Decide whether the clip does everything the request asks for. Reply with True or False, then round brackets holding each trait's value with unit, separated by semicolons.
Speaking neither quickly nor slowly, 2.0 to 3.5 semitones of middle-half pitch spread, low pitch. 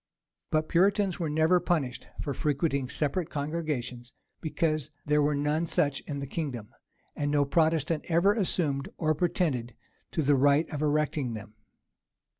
False (145 wpm; 2.7 semitones; 150 Hz)